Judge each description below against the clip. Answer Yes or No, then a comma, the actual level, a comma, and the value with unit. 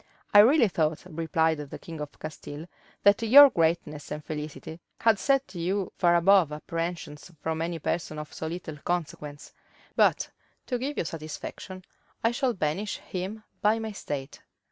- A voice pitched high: No, medium, 170 Hz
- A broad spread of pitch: No, average, 4.8 semitones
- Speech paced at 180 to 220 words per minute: No, average, 150 wpm